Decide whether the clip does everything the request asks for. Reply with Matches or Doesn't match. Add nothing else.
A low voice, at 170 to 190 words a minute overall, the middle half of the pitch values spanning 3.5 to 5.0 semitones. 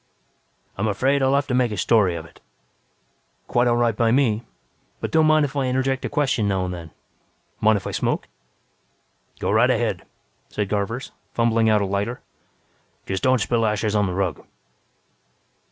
Matches